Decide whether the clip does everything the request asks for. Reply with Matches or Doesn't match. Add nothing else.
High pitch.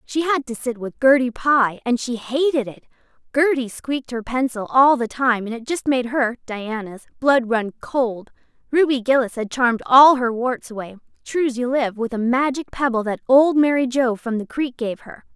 Matches